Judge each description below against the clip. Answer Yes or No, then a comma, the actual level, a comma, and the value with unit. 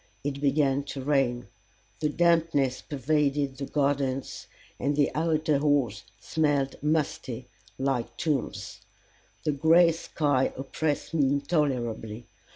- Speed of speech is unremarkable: No, slow, 110 wpm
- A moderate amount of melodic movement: No, narrow, 2.3 semitones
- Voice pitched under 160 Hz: Yes, medium, 140 Hz